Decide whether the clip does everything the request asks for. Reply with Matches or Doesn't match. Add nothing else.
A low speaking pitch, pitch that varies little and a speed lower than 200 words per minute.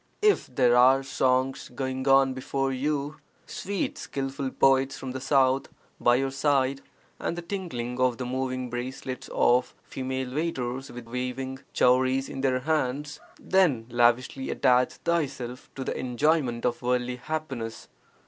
Matches